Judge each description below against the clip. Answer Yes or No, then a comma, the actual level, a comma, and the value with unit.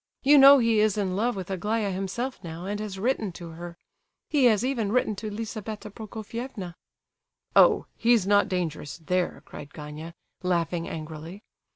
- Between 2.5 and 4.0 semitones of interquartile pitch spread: No, average, 4.4 semitones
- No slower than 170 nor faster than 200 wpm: No, average, 160 wpm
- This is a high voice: Yes, high, 200 Hz